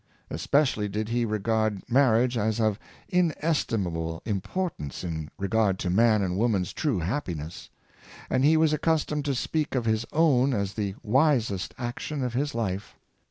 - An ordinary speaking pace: Yes, average, 155 wpm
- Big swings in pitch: Yes, wide, 5.9 semitones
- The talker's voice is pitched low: Yes, low, 115 Hz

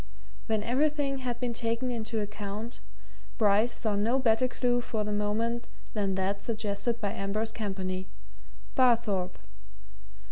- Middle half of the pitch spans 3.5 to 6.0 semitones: No, average, 2.7 semitones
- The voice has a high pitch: Yes, high, 220 Hz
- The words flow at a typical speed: No, slow, 130 wpm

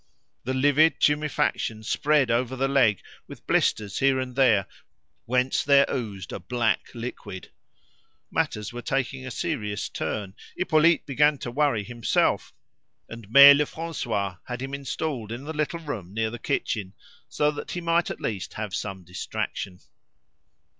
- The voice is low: Yes, low, 125 Hz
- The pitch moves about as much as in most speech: Yes, average, 4.9 semitones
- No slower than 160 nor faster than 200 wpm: No, average, 145 wpm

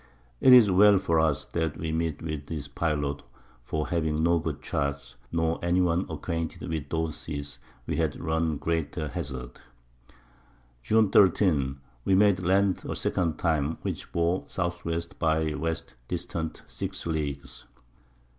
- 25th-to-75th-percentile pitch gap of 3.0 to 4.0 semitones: No, narrow, 2.4 semitones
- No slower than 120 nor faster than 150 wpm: Yes, average, 145 wpm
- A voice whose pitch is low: Yes, very low, 80 Hz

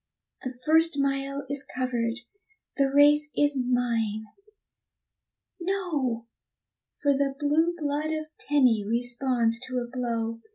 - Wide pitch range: No, average, 3.4 semitones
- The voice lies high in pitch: Yes, very high, 270 Hz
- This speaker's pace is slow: Yes, slow, 115 wpm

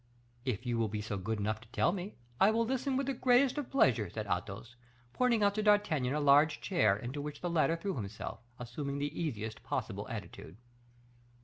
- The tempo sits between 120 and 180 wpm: No, average, 195 wpm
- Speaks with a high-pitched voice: No, medium, 145 Hz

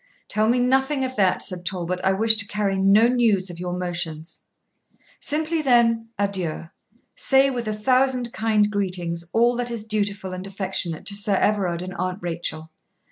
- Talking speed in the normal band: Yes, average, 170 wpm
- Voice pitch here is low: No, high, 205 Hz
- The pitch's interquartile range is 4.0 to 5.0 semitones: Yes, average, 4.4 semitones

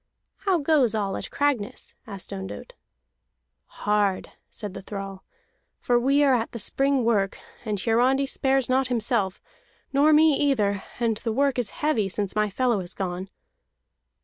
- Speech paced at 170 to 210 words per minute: No, average, 150 wpm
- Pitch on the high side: Yes, high, 230 Hz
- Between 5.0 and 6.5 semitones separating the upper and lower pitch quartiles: Yes, average, 5.3 semitones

